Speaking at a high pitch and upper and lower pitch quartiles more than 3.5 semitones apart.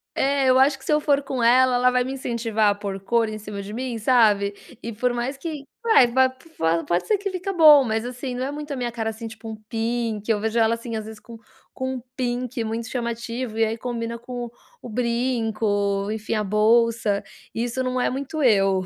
No: high, 235 Hz; average, 2.9 semitones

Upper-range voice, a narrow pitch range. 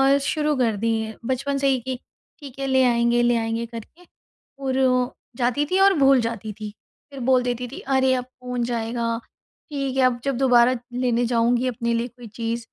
Yes: high, 245 Hz; narrow, 2.2 semitones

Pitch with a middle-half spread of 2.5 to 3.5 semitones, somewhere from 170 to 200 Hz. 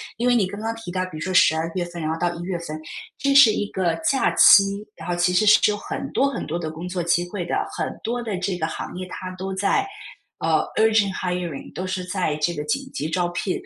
Yes: average, 3.1 semitones; medium, 185 Hz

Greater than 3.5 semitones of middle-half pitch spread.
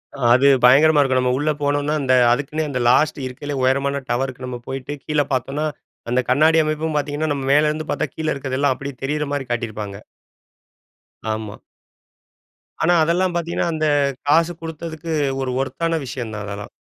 No: average, 3.2 semitones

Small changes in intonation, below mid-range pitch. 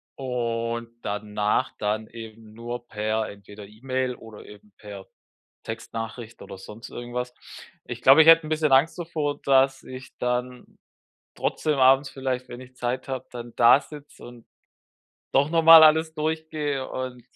No: average, 3.3 semitones; low, 125 Hz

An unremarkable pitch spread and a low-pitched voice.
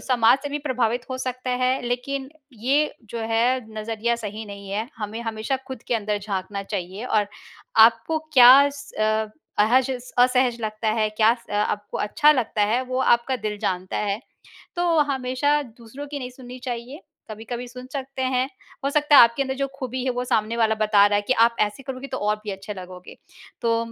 No: average, 3.2 semitones; high, 235 Hz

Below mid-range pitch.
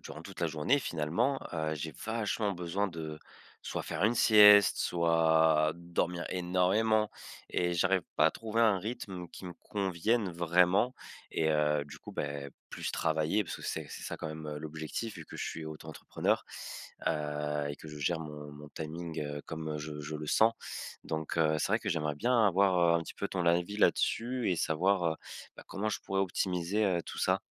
Yes: very low, 85 Hz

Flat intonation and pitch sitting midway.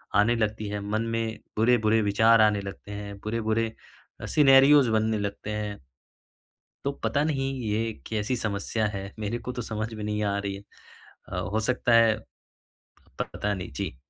No: narrow, 1.9 semitones; low, 110 Hz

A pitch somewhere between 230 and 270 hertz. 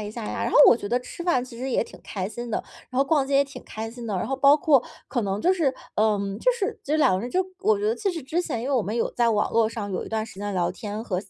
Yes: high, 240 Hz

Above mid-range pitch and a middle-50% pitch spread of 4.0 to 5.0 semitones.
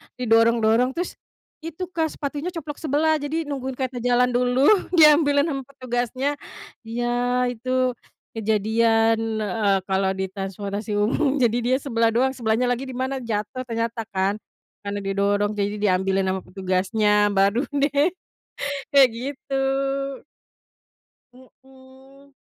Yes: high, 245 Hz; average, 4.3 semitones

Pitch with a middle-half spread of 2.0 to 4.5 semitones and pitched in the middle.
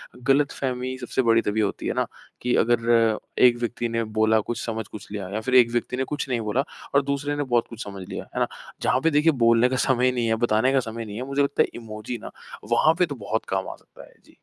No: average, 2.8 semitones; low, 120 Hz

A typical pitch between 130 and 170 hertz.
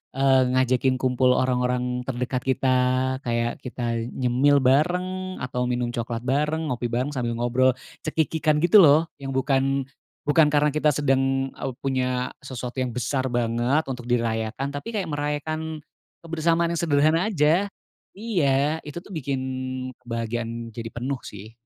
Yes: low, 135 Hz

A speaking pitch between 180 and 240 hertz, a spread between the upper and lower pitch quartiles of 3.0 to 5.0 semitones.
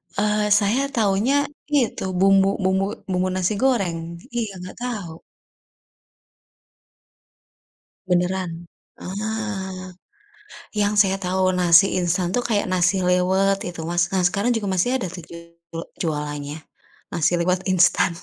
No: medium, 185 Hz; narrow, 2.4 semitones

